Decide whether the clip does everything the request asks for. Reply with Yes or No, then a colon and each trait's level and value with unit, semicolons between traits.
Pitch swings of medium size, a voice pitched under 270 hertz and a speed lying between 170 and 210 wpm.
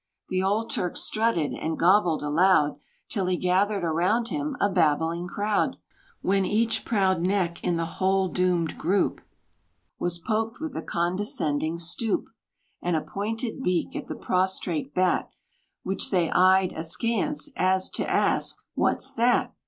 No: average, 3.5 semitones; medium, 185 Hz; average, 145 wpm